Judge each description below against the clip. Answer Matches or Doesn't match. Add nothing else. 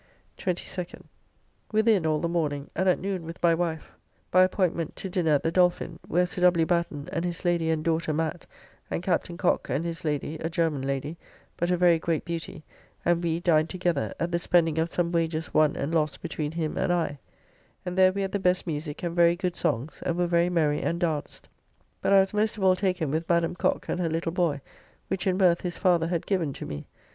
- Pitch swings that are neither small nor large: Doesn't match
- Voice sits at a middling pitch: Matches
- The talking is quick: Matches